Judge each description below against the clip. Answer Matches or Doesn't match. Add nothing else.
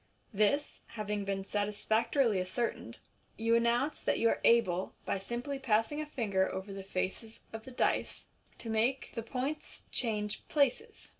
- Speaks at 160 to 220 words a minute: Doesn't match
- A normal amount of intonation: Matches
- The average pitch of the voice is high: Matches